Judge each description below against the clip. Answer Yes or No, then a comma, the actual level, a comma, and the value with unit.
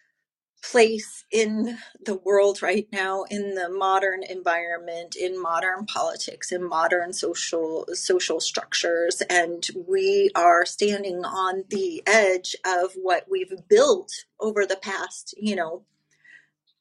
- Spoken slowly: Yes, slow, 120 wpm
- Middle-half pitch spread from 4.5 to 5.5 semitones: No, average, 3.7 semitones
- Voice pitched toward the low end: No, high, 190 Hz